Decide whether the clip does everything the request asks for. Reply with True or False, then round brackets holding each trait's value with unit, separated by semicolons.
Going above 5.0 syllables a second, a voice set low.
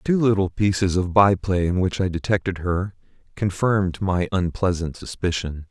False (4.9 syllables/s; 95 Hz)